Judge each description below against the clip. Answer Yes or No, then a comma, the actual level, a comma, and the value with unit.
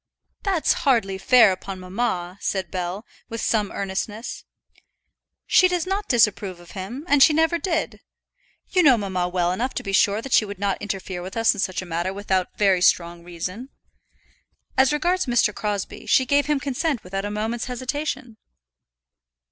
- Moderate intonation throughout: No, wide, 6.0 semitones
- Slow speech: No, average, 170 wpm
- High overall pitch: Yes, high, 210 Hz